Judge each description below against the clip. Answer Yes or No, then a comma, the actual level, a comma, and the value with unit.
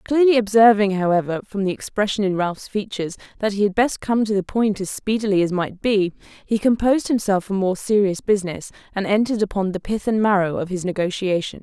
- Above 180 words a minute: Yes, average, 200 wpm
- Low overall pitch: No, high, 200 Hz